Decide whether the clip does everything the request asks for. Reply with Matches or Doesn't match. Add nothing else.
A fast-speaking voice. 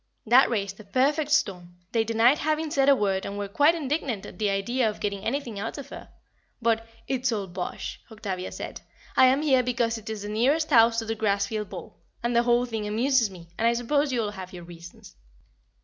Matches